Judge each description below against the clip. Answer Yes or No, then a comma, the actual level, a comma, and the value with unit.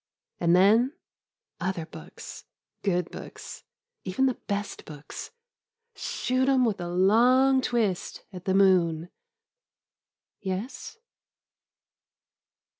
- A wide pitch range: Yes, wide, 6.1 semitones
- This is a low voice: No, high, 200 Hz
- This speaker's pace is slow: Yes, slow, 110 wpm